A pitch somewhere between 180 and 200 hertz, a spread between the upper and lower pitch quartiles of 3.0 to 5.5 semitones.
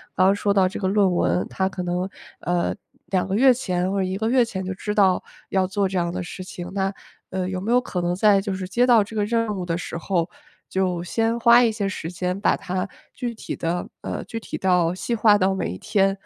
No: high, 190 Hz; narrow, 2.6 semitones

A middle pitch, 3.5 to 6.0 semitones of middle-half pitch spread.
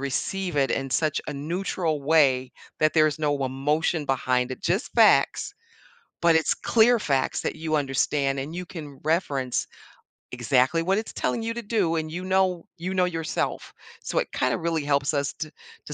Yes: medium, 155 Hz; average, 4.1 semitones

